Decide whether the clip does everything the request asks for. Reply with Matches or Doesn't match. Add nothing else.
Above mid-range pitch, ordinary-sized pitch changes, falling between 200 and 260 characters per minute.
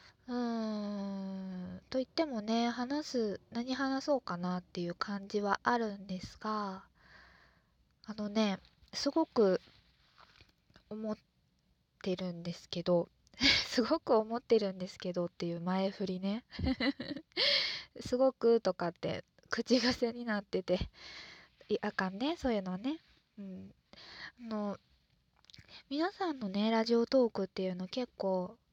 Matches